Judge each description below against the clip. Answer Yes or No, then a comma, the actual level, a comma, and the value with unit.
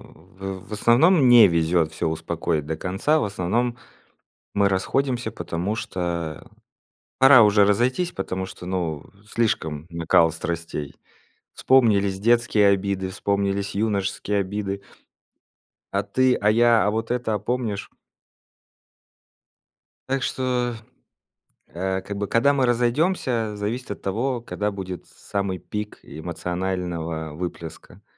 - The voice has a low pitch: Yes, low, 100 Hz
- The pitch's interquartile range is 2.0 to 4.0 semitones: No, average, 4.5 semitones